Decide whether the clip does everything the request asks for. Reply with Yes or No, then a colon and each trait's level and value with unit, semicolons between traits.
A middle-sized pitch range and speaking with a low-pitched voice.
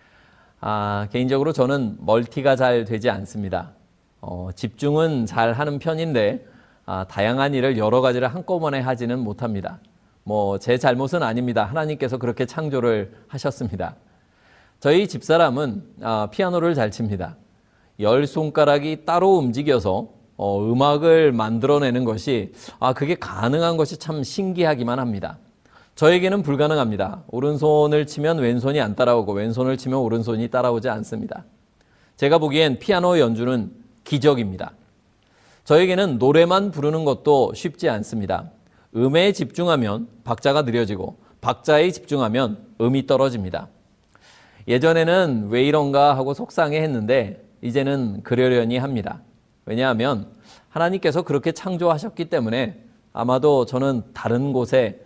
Yes: average, 5.0 semitones; low, 130 Hz